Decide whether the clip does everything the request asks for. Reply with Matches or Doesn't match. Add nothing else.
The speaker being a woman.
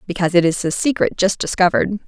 Matches